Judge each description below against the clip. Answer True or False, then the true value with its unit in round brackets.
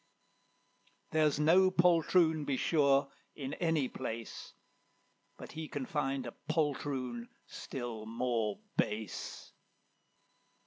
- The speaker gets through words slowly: True (95 wpm)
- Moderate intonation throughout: True (4.5 semitones)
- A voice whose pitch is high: False (140 Hz)